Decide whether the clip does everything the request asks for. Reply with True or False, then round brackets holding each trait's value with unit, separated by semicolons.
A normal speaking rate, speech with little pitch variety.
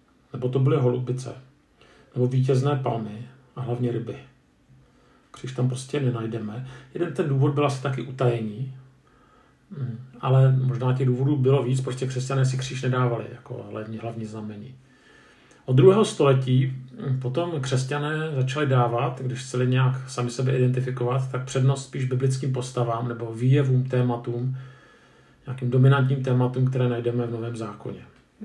True (135 wpm; 1.4 semitones)